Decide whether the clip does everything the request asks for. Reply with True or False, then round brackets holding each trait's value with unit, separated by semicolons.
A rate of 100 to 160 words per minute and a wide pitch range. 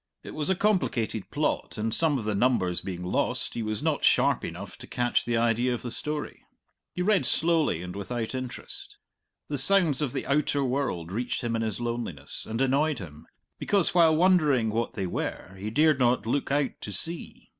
False (195 wpm; 5.7 semitones)